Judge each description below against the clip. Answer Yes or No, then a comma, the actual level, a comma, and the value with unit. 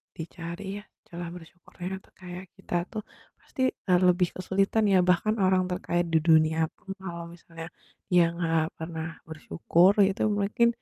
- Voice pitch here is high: No, medium, 180 Hz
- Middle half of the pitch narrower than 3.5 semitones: Yes, narrow, 2.4 semitones